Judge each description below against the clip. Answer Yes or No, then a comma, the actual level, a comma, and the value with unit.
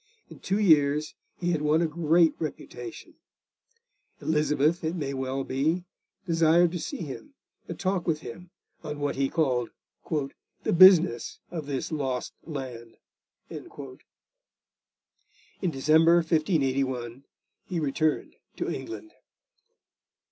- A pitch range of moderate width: Yes, average, 3.8 semitones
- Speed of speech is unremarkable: No, slow, 115 wpm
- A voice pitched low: No, medium, 155 Hz